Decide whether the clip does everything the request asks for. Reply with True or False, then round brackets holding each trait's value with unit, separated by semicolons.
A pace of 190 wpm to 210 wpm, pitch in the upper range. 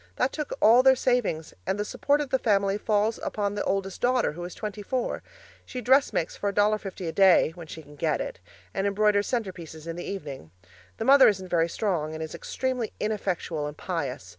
True (200 wpm; 200 Hz)